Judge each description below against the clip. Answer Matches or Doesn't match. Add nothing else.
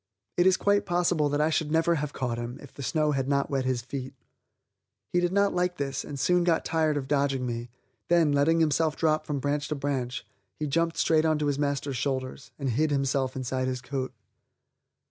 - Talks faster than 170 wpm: Matches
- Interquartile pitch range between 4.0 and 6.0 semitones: Doesn't match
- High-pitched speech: Doesn't match